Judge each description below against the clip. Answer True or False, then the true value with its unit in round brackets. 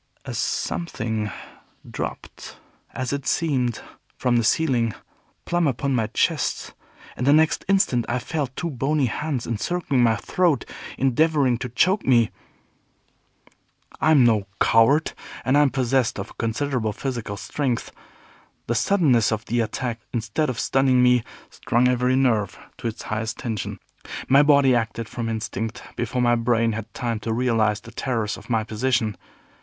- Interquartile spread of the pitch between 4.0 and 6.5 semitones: False (3.3 semitones)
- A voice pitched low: True (125 Hz)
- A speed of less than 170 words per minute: True (150 wpm)